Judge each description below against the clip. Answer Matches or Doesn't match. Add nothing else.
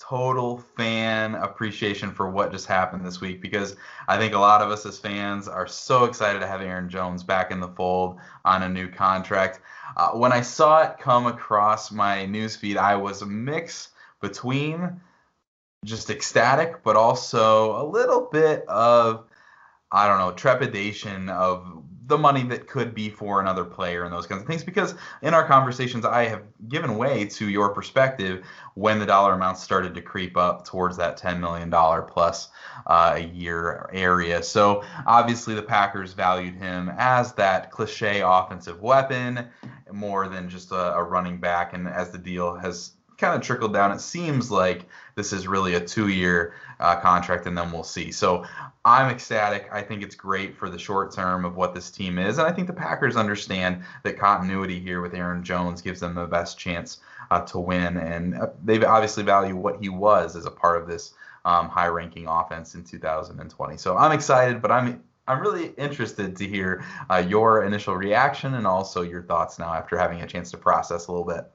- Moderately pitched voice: Doesn't match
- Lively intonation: Doesn't match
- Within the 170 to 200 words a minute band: Matches